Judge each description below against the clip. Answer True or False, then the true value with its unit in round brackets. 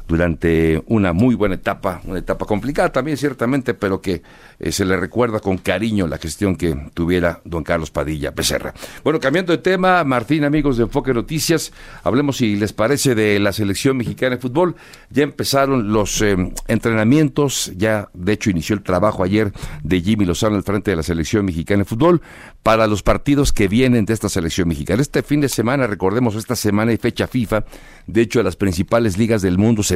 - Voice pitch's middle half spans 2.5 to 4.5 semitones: False (4.9 semitones)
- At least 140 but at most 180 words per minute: False (190 wpm)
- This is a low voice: True (110 Hz)